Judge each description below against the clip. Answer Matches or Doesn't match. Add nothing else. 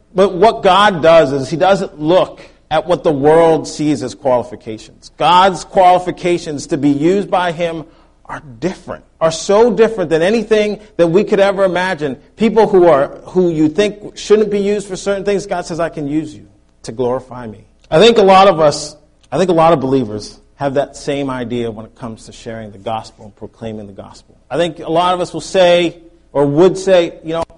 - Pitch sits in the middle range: Matches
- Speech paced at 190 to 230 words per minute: Matches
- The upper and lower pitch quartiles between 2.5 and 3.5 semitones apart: Doesn't match